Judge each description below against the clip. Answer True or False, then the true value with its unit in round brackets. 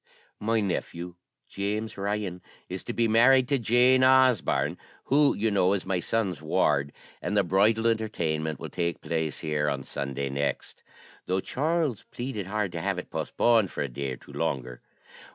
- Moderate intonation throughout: False (6.3 semitones)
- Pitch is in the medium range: False (100 Hz)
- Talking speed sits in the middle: True (170 wpm)